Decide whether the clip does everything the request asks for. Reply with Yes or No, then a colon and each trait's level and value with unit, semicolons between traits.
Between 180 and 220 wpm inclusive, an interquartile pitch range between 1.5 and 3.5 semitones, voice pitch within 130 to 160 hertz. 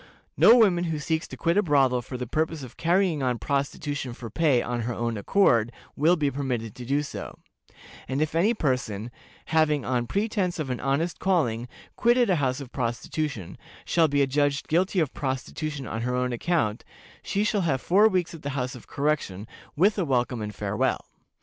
No: average, 190 wpm; average, 5.1 semitones; medium, 140 Hz